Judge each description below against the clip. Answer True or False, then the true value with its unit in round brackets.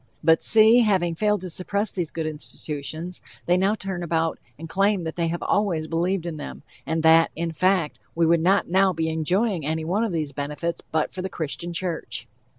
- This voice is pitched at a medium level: True (170 Hz)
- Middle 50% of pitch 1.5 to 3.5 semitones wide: True (2.8 semitones)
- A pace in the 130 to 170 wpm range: False (200 wpm)